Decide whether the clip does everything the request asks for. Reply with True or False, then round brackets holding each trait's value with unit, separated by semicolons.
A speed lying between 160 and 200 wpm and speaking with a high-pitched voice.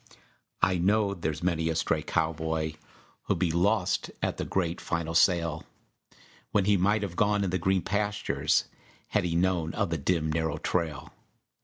False (165 wpm; 85 Hz)